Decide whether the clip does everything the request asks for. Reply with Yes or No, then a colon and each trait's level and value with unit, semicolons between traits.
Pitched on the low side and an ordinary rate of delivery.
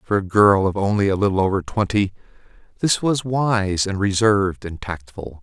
Yes: low, 100 Hz; average, 175 wpm